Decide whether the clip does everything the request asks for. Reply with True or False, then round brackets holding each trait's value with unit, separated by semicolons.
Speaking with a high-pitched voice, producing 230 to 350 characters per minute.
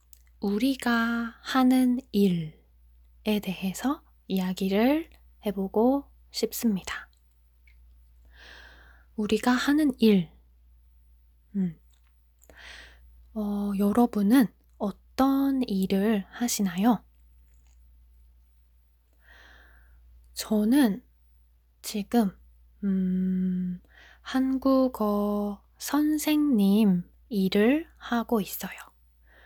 False (195 Hz; 120 characters per minute)